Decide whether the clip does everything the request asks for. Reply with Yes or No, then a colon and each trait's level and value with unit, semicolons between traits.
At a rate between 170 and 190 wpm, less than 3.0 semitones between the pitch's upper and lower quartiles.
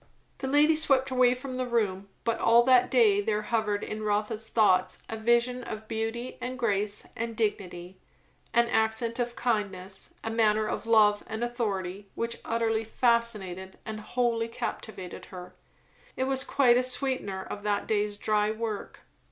No: average, 160 wpm; narrow, 2.5 semitones